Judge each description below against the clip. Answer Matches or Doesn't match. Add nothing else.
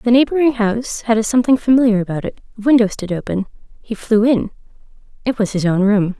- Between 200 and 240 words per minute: Matches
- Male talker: Doesn't match